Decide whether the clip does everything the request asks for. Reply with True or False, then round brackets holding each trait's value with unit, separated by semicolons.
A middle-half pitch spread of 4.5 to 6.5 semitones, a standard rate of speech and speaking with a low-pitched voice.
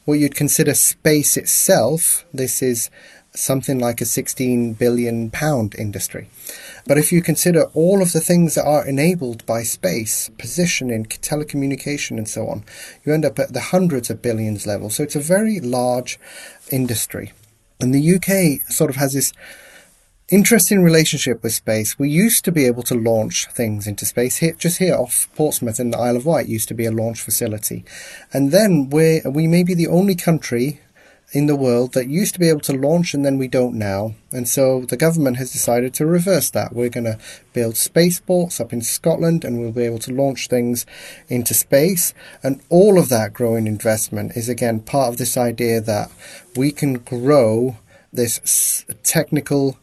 True (5.1 semitones; 185 wpm; 130 Hz)